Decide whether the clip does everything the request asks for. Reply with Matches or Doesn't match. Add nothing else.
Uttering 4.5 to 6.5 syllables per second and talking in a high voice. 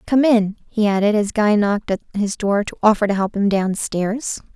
Matches